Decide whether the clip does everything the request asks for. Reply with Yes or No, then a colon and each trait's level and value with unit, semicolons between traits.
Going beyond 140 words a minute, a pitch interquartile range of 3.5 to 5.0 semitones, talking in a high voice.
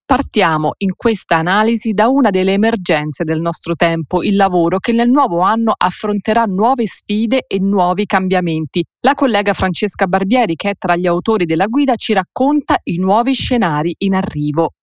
Yes: average, 165 wpm; average, 4.6 semitones; high, 195 Hz